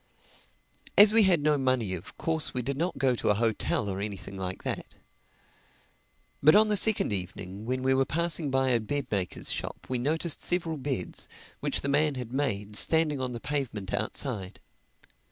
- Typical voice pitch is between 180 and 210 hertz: No, low, 130 Hz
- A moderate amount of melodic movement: No, wide, 6.5 semitones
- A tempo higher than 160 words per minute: Yes, average, 180 wpm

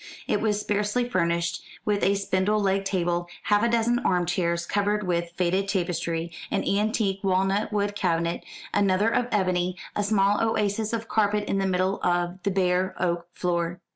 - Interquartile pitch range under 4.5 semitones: Yes, average, 2.8 semitones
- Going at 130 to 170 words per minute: Yes, average, 165 wpm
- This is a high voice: Yes, high, 195 Hz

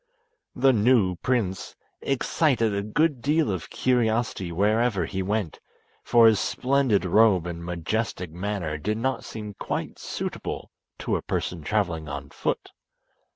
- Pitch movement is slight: No, average, 5.0 semitones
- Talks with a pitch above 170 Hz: No, low, 105 Hz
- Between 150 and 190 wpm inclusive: No, average, 140 wpm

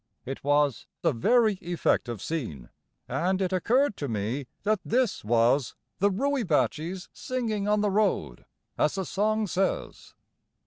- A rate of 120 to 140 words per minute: Yes, slow, 135 wpm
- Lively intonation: Yes, wide, 7.1 semitones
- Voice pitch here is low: No, medium, 185 Hz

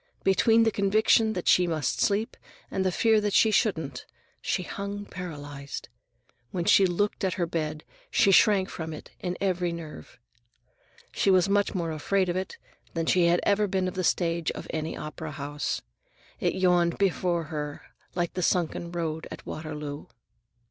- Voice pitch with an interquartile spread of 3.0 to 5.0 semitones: Yes, average, 3.5 semitones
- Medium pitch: Yes, medium, 175 Hz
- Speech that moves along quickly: No, average, 170 wpm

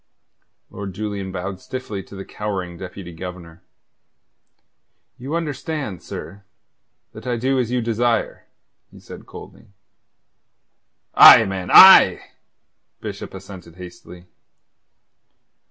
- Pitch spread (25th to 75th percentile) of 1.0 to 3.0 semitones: No, average, 4.8 semitones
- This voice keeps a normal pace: No, slow, 105 wpm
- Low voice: Yes, low, 100 Hz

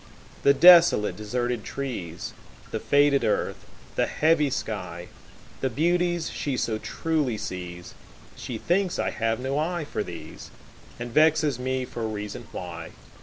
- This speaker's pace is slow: Yes, slow, 120 wpm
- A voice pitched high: No, low, 125 Hz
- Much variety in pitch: Yes, wide, 6.3 semitones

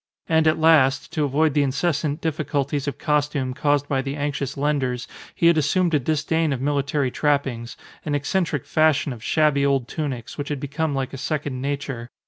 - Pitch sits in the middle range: Yes, medium, 145 Hz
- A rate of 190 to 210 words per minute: No, average, 180 wpm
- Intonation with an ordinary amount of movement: No, narrow, 2.2 semitones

